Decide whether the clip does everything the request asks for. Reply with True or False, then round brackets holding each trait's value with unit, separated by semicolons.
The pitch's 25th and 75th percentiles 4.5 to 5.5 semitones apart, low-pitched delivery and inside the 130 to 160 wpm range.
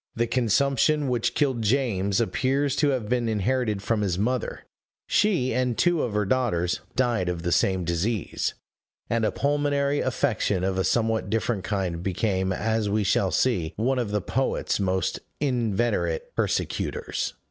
True (4.9 semitones; 115 Hz; 155 wpm)